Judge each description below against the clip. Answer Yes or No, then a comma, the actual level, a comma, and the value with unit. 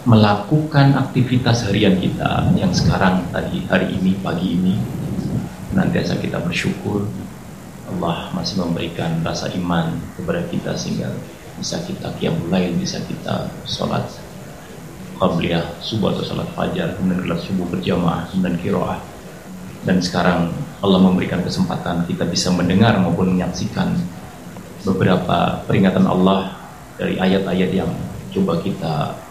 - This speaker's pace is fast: No, average, 120 wpm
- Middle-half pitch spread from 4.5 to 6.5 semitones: No, average, 2.7 semitones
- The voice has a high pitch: No, very low, 95 Hz